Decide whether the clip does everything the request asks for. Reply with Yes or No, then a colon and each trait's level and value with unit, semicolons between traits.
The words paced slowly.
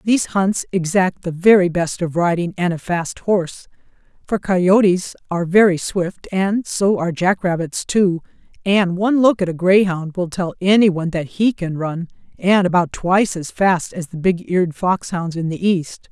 No: average, 180 wpm